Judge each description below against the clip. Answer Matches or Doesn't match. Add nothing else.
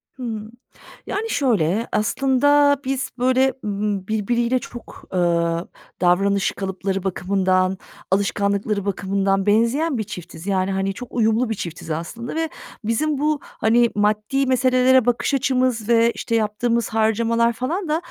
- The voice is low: Doesn't match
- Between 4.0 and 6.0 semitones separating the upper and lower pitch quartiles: Matches